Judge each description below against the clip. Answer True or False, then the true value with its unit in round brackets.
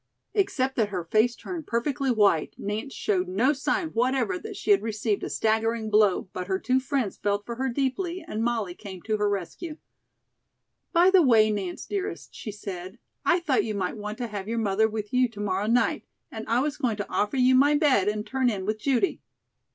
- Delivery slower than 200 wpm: False (205 wpm)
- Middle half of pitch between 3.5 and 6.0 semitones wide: True (4.5 semitones)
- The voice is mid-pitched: False (225 Hz)